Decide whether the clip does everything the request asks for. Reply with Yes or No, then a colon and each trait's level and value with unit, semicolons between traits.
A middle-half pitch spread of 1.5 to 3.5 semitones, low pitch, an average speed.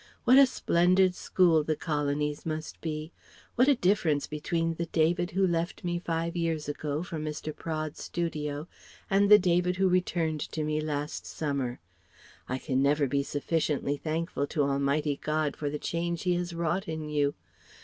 No: narrow, 2.6 semitones; medium, 160 Hz; average, 170 wpm